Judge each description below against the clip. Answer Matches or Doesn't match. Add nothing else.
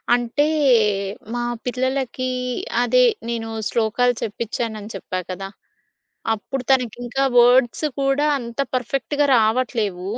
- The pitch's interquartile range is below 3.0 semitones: Matches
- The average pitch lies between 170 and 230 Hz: Doesn't match